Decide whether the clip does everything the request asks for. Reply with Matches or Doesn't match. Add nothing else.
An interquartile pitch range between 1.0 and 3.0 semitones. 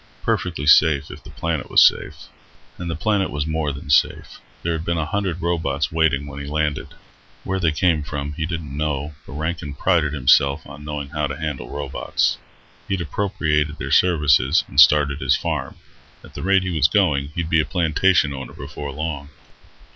Matches